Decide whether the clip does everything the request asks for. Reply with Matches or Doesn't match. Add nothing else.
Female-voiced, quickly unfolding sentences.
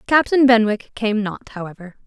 Doesn't match